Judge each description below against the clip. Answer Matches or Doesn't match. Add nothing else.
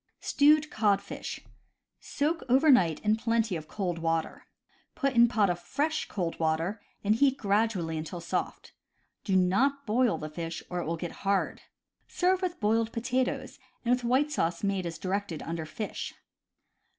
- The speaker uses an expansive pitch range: Matches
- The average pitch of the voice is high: Matches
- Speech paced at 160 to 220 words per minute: Matches